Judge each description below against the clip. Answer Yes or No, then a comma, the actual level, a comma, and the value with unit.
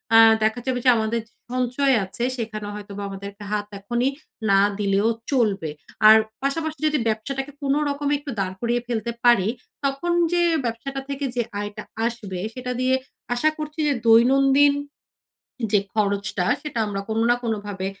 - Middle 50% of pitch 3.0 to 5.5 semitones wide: Yes, average, 4.8 semitones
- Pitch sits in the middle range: No, high, 235 Hz